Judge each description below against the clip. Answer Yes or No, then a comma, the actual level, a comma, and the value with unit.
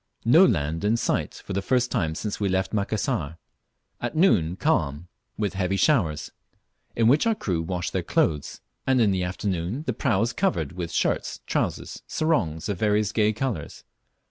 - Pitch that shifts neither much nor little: No, wide, 5.8 semitones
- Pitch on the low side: Yes, low, 100 Hz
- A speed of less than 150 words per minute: No, average, 175 wpm